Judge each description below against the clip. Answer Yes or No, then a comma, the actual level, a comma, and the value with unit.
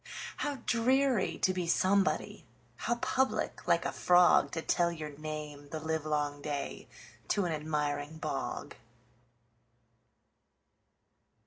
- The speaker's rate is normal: No, slow, 95 wpm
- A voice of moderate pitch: Yes, medium, 160 Hz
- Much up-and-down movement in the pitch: No, average, 3.8 semitones